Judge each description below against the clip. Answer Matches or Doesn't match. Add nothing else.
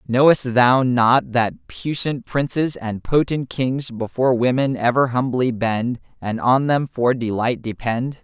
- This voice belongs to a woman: Doesn't match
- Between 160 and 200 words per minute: Doesn't match